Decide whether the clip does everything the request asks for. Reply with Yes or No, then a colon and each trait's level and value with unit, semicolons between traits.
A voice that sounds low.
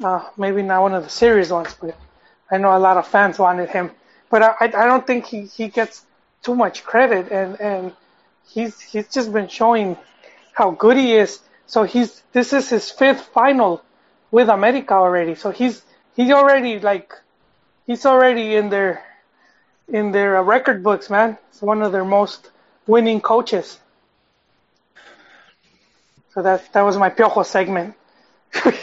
No: high, 215 Hz